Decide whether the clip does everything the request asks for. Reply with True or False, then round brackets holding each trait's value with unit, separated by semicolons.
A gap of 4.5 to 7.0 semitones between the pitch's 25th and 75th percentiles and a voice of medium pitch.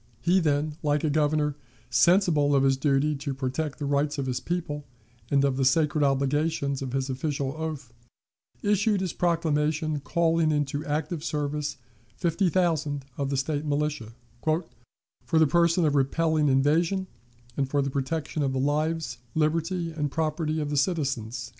False (2.5 semitones; 150 Hz)